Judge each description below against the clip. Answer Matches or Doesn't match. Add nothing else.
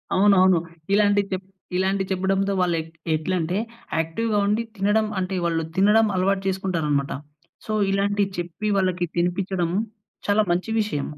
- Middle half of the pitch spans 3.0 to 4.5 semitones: Doesn't match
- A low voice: Doesn't match